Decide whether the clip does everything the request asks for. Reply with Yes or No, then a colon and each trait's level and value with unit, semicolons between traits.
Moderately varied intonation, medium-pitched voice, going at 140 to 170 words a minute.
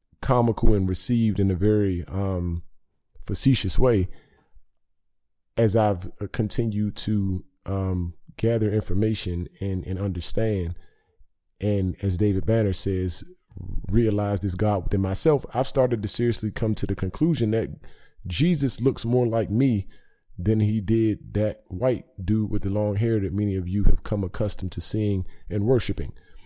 No: average, 3.0 semitones; low, 105 Hz; average, 145 wpm